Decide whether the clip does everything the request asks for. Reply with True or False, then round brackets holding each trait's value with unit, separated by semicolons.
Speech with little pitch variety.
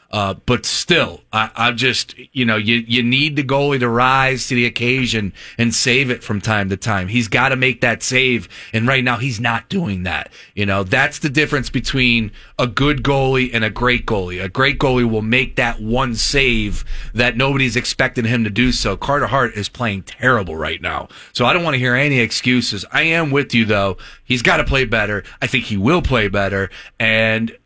False (3.0 semitones)